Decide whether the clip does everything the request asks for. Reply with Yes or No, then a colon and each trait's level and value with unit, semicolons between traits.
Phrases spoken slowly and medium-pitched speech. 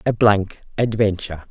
No: slow, 120 wpm; low, 105 Hz